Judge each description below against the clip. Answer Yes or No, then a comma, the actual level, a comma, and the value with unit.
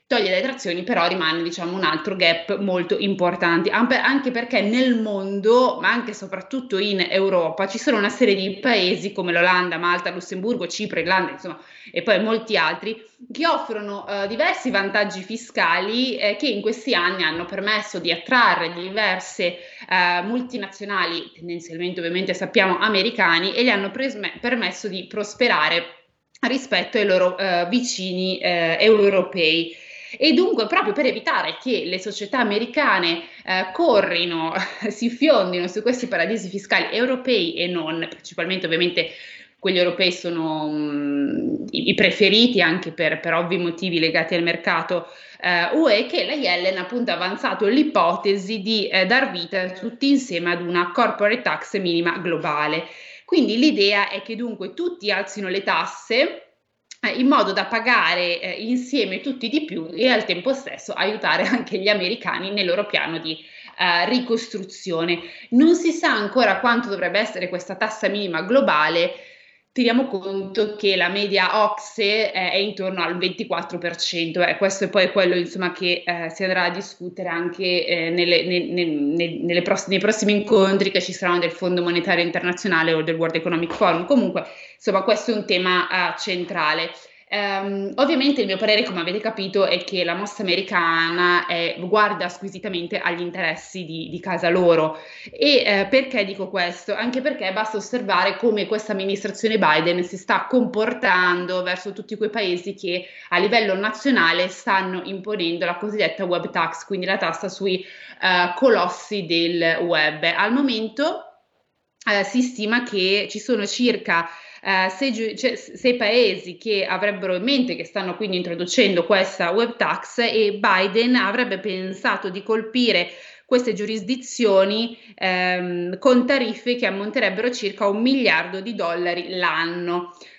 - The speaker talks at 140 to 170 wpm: Yes, average, 155 wpm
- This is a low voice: No, high, 195 Hz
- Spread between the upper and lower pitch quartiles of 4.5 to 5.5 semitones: No, average, 4.1 semitones